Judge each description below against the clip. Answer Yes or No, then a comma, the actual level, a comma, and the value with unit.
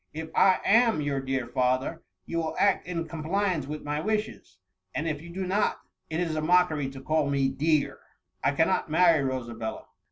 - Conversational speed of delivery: No, fast, 210 wpm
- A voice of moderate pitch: Yes, medium, 155 Hz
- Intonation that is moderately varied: Yes, average, 4.6 semitones